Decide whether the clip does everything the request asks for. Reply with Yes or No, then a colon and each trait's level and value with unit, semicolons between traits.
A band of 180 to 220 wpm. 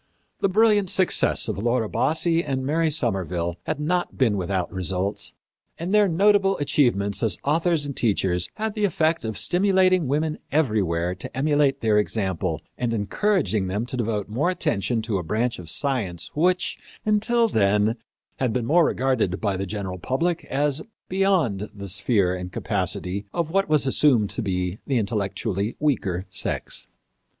No: average, 155 wpm